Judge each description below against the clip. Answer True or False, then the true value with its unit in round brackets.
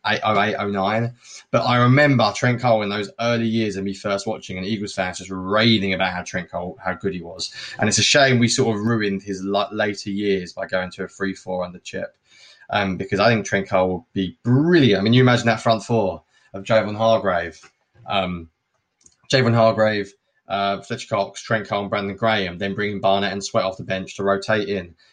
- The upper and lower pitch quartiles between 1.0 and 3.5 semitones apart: True (2.9 semitones)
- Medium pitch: False (100 Hz)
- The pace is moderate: False (210 wpm)